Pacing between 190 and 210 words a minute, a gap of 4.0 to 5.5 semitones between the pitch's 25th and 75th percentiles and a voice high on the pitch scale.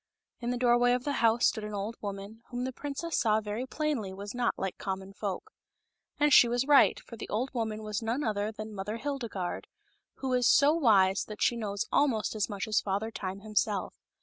No: fast, 205 wpm; average, 3.4 semitones; high, 220 Hz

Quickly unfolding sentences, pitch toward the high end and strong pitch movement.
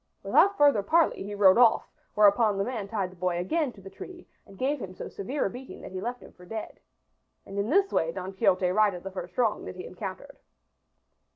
No: fast, 220 wpm; high, 200 Hz; average, 4.9 semitones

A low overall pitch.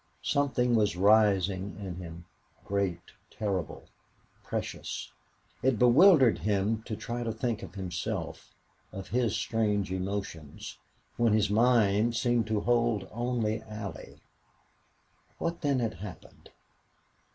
Yes: low, 105 Hz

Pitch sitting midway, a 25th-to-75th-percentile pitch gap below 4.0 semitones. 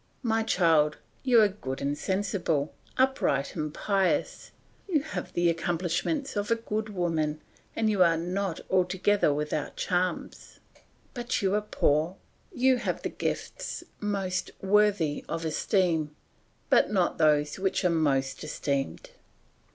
No: medium, 180 Hz; average, 5.2 semitones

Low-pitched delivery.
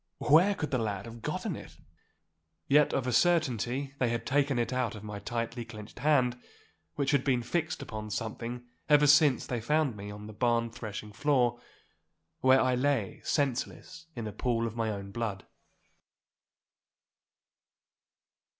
Yes: low, 120 Hz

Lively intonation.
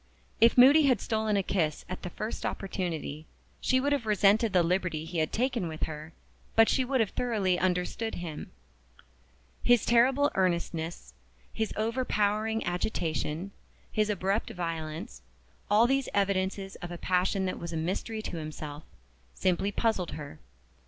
No: average, 4.6 semitones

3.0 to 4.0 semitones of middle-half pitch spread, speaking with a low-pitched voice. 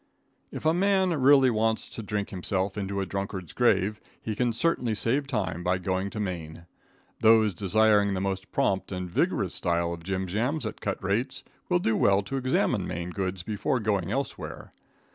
Yes: average, 3.7 semitones; low, 100 Hz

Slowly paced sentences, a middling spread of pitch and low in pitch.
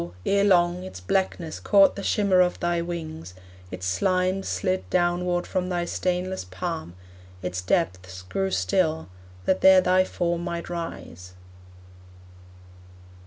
No: slow, 125 wpm; average, 3.0 semitones; medium, 175 Hz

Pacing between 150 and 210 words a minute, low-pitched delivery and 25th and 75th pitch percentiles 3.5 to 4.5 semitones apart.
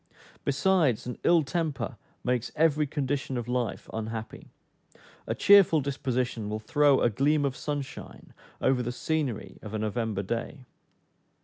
No: slow, 135 wpm; low, 130 Hz; average, 4.1 semitones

